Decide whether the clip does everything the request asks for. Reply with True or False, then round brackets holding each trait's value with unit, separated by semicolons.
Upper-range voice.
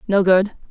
True (195 Hz)